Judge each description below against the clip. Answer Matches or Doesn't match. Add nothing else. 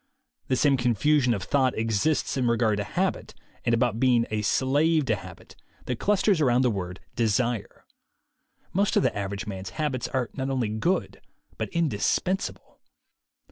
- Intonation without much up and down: Doesn't match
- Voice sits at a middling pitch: Doesn't match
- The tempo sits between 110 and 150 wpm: Doesn't match